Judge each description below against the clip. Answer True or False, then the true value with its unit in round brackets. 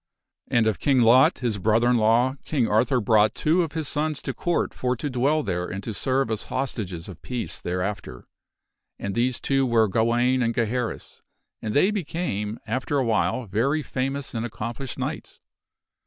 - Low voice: True (120 Hz)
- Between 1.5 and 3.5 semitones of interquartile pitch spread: False (3.9 semitones)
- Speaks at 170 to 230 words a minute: True (175 wpm)